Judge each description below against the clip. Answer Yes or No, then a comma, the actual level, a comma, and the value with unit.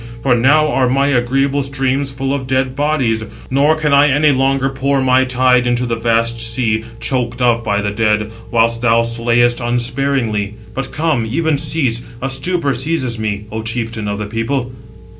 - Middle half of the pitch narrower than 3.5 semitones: Yes, average, 2.8 semitones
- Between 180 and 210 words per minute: No, average, 165 wpm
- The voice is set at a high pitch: No, low, 125 Hz